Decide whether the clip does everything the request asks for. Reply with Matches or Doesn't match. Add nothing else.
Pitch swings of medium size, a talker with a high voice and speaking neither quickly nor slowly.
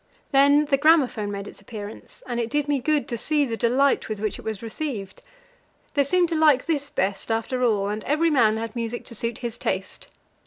Doesn't match